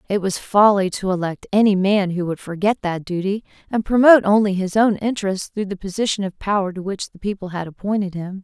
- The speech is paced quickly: Yes, fast, 215 wpm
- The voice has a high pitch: Yes, high, 195 Hz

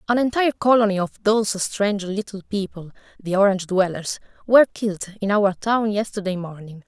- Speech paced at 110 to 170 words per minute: Yes, average, 155 wpm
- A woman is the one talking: Yes, female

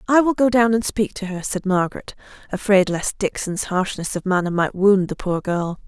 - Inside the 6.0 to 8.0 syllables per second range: No, 5.1 syllables/s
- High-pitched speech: Yes, high, 195 Hz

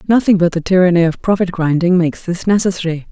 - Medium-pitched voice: Yes, medium, 180 Hz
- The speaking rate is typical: Yes, average, 195 wpm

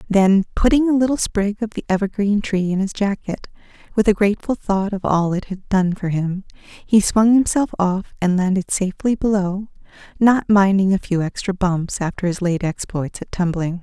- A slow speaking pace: No, average, 185 wpm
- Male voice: No, female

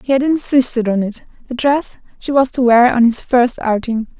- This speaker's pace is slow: No, average, 200 wpm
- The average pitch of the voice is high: Yes, high, 245 Hz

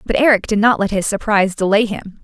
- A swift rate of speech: Yes, fast, 240 wpm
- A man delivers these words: No, female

